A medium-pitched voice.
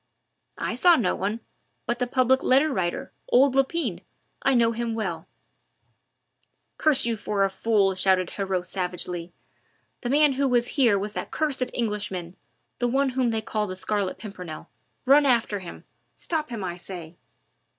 No: high, 225 Hz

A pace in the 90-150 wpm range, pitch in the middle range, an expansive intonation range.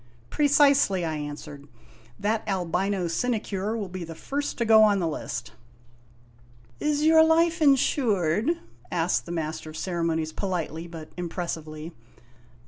Yes: average, 145 wpm; medium, 175 Hz; wide, 6.2 semitones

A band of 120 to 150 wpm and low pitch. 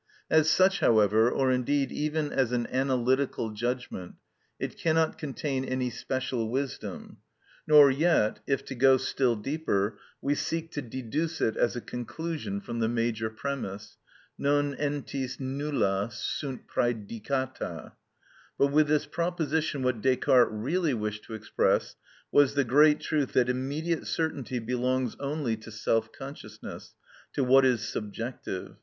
Yes: slow, 135 wpm; low, 130 Hz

